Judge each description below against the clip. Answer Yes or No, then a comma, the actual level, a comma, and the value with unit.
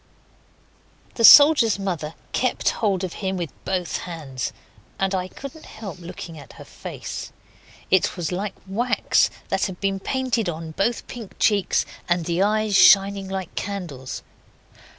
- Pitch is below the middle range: No, high, 190 Hz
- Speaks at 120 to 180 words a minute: Yes, average, 145 wpm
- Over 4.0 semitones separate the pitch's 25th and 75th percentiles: No, average, 3.5 semitones